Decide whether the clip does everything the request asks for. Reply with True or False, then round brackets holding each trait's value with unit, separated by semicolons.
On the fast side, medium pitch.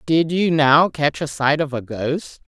True (210 wpm; 150 Hz)